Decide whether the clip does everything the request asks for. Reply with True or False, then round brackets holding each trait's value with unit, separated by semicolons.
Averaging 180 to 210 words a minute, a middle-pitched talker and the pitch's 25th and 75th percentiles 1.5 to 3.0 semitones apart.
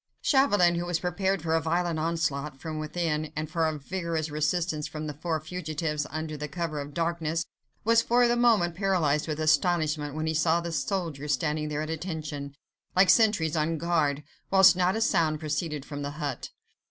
True (185 wpm; 160 Hz; 2.5 semitones)